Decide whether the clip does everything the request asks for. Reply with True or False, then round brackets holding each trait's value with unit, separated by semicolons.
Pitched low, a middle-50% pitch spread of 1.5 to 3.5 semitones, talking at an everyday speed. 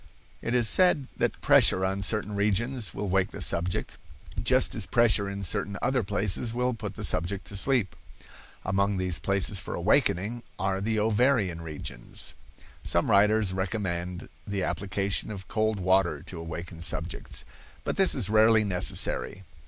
True (100 Hz; 2.9 semitones; 155 wpm)